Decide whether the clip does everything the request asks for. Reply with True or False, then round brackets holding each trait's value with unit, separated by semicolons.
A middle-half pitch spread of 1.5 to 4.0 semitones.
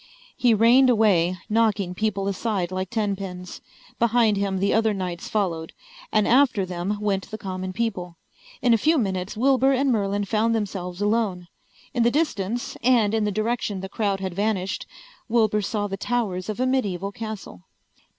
True (3.3 semitones)